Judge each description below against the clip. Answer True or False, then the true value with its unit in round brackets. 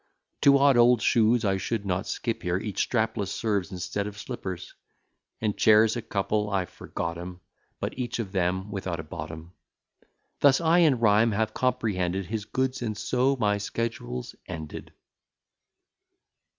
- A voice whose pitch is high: False (105 Hz)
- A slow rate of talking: False (150 wpm)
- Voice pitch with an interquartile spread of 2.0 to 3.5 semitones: False (4.2 semitones)